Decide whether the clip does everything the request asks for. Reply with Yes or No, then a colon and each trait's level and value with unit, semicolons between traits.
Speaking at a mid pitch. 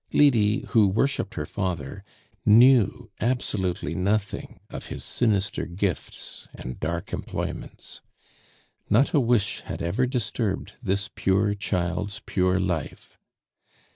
No: low, 100 Hz